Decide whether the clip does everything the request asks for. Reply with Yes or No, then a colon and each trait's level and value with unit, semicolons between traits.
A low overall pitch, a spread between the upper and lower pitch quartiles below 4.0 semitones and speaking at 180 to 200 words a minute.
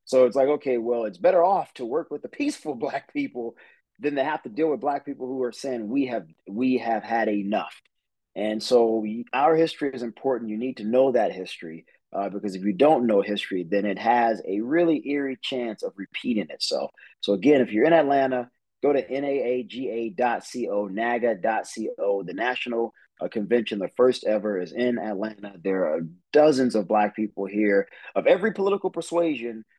No: low, 120 Hz; average, 4.7 semitones; average, 185 wpm